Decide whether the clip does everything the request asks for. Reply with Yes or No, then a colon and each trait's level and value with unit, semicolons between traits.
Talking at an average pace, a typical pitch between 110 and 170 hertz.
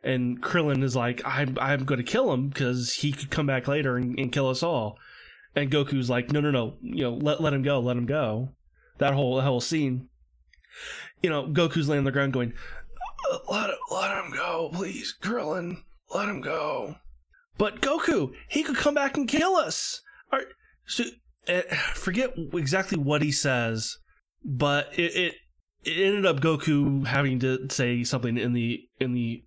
Yes: average, 185 wpm; medium, 140 Hz